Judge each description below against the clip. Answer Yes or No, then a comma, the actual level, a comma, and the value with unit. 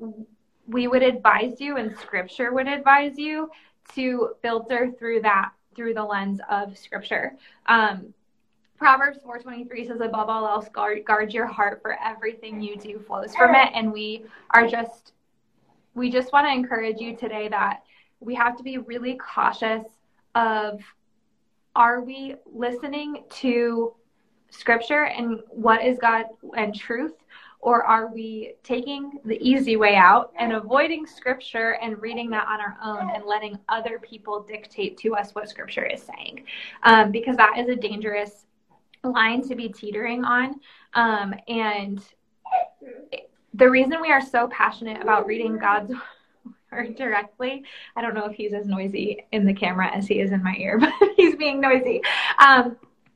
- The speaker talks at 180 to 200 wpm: No, average, 155 wpm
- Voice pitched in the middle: No, high, 230 Hz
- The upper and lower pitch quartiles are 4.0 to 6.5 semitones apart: No, average, 2.9 semitones